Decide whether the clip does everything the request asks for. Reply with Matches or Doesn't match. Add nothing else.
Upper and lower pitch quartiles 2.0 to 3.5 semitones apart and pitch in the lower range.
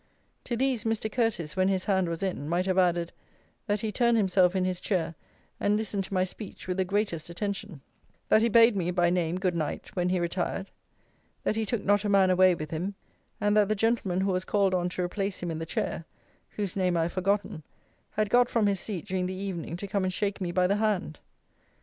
Doesn't match